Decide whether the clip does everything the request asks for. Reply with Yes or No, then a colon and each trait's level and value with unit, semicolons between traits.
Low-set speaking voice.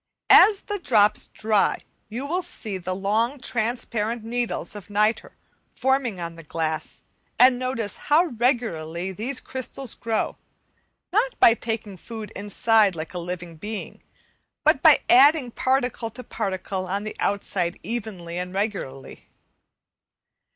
No: high, 220 Hz